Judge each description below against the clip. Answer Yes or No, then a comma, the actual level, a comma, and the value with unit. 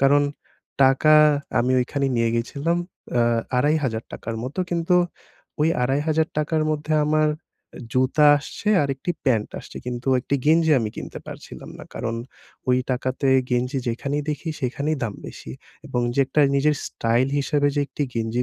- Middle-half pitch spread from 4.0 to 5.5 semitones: No, average, 3.6 semitones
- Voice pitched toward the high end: No, medium, 140 Hz